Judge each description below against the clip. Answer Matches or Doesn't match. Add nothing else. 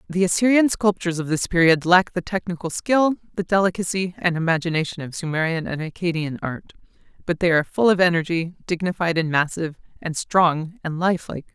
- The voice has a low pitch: Doesn't match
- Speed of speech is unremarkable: Matches